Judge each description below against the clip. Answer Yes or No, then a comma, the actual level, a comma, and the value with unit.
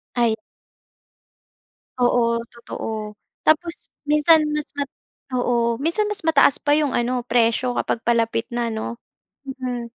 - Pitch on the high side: Yes, high, 245 Hz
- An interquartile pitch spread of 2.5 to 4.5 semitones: Yes, average, 4.0 semitones